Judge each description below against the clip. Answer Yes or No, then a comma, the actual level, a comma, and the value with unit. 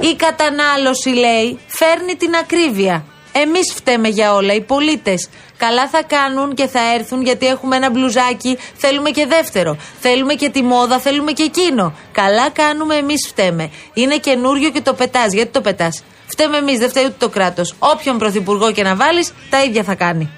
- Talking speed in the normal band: No, fast, 175 wpm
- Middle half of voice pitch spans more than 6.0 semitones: No, wide, 5.4 semitones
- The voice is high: Yes, very high, 260 Hz